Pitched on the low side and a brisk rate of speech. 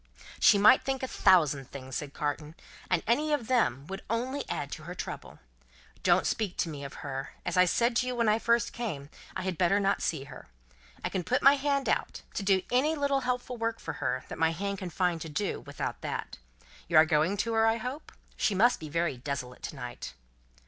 No: high, 195 Hz; fast, 220 wpm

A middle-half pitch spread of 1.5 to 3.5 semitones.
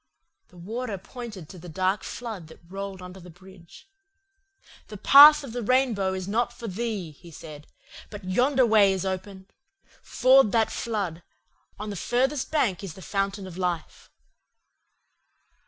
No: average, 4.4 semitones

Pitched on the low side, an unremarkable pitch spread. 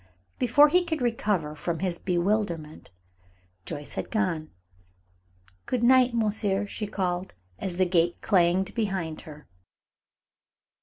No: high, 190 Hz; average, 4.3 semitones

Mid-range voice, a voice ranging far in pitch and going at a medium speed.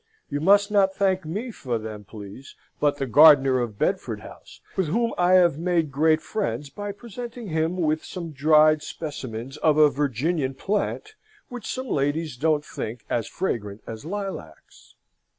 Yes: medium, 155 Hz; wide, 6.0 semitones; average, 160 wpm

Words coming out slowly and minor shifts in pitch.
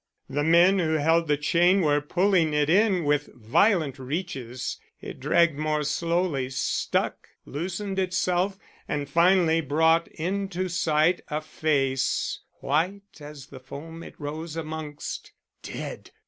No: slow, 130 wpm; average, 3.3 semitones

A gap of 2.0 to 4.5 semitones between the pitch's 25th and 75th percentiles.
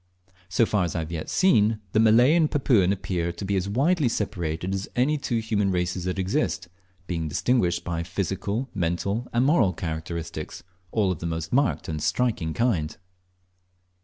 No: wide, 5.5 semitones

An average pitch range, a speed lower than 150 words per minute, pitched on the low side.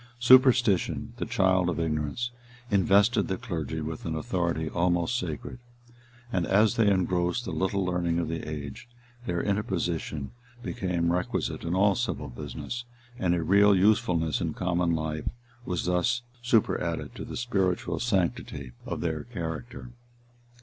Yes: average, 3.8 semitones; average, 140 wpm; very low, 90 Hz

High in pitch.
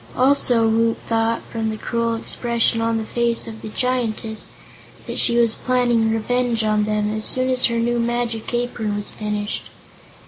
Yes: high, 230 Hz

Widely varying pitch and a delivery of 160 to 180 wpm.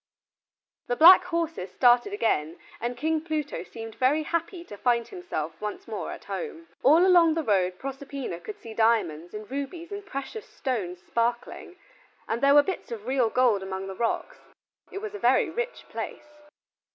Yes: wide, 7.1 semitones; average, 170 wpm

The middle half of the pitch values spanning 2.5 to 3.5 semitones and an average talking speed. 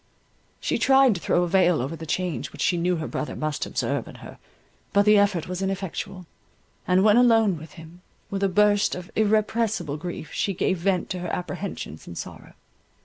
Yes: average, 3.0 semitones; average, 195 wpm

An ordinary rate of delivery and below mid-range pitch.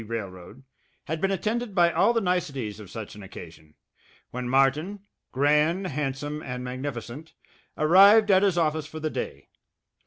No: average, 150 wpm; medium, 150 Hz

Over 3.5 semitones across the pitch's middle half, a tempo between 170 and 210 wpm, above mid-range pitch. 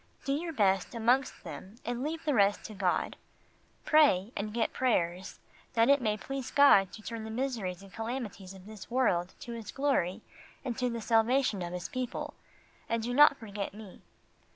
Yes: average, 4.6 semitones; average, 180 wpm; high, 225 Hz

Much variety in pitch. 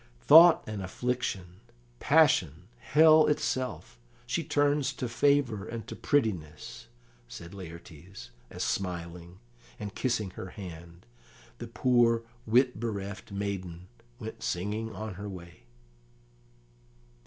Yes: wide, 6.0 semitones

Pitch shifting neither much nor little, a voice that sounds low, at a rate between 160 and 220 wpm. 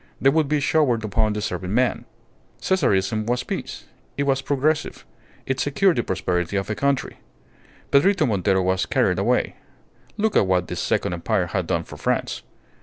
No: wide, 6.9 semitones; low, 115 Hz; average, 165 wpm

